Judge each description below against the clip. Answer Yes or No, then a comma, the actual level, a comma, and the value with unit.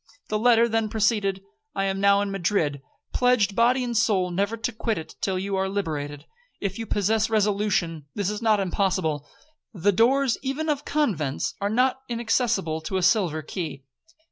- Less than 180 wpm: Yes, average, 170 wpm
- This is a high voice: Yes, high, 205 Hz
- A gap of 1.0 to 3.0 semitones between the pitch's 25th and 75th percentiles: No, average, 3.6 semitones